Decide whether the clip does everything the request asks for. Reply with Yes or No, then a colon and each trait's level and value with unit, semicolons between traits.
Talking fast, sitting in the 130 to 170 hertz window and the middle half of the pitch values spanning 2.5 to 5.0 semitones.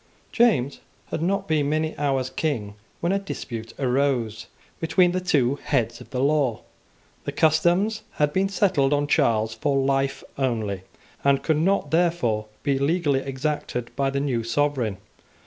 No: average, 150 wpm; medium, 140 Hz; average, 4.2 semitones